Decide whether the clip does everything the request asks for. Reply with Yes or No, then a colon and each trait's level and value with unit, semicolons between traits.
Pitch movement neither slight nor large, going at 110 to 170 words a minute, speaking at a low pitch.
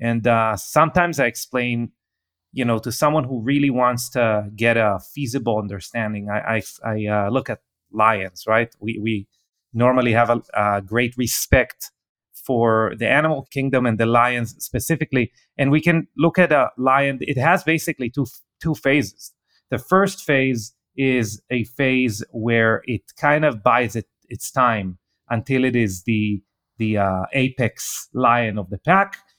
Yes: average, 3.5 semitones; average, 160 wpm; low, 120 Hz